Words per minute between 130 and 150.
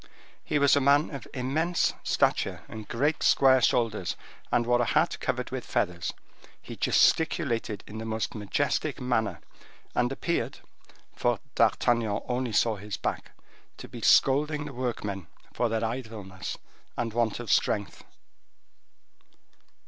Yes: slow, 135 wpm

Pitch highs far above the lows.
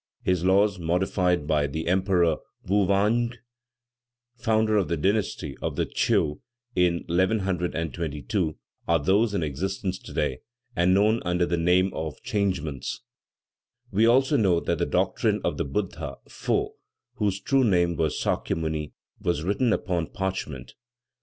No: average, 3.6 semitones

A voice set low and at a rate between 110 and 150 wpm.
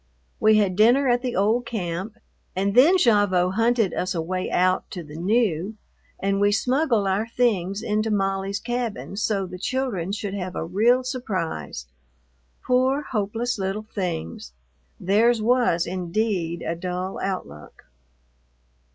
No: high, 200 Hz; average, 140 wpm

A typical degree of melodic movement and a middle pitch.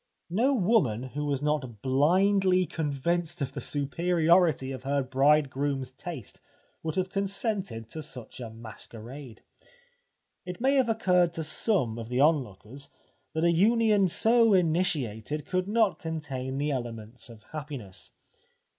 No: wide, 5.9 semitones; medium, 150 Hz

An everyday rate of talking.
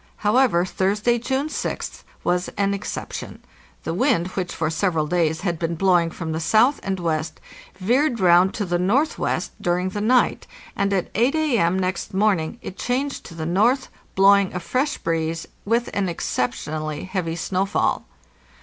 Yes: average, 160 wpm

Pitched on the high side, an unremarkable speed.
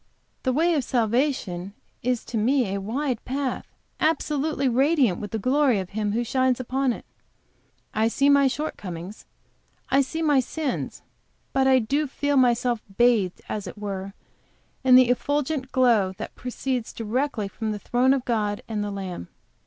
Yes: very high, 250 Hz; average, 160 wpm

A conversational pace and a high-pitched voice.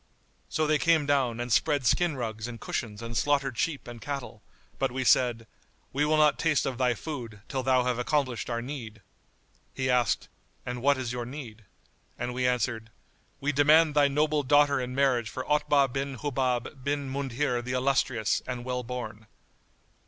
No: average, 175 wpm; low, 130 Hz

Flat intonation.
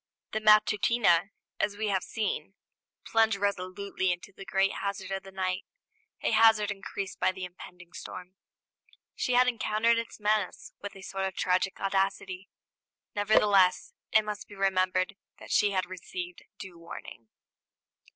Yes: narrow, 2.2 semitones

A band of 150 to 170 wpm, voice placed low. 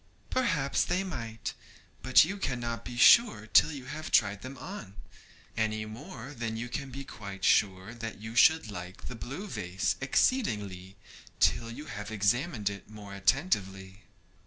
Yes: average, 155 wpm; low, 115 Hz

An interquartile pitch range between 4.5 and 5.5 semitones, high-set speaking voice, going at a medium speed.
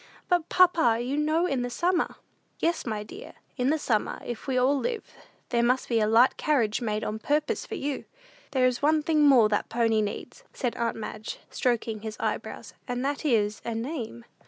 Yes: average, 5.0 semitones; very high, 250 Hz; average, 195 wpm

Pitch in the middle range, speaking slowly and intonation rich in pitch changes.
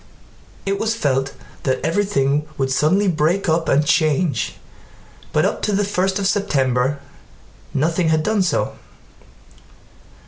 Yes: medium, 160 Hz; slow, 130 wpm; wide, 5.9 semitones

